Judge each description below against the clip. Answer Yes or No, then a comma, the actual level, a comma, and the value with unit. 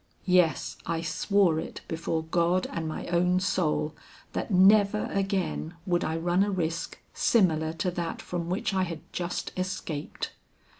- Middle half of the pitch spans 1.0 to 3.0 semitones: Yes, narrow, 2.4 semitones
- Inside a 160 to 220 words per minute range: No, average, 150 wpm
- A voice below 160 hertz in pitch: No, medium, 175 Hz